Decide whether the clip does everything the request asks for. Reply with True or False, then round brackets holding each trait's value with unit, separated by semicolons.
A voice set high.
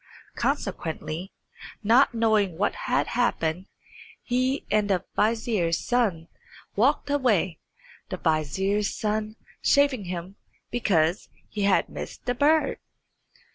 True (210 Hz)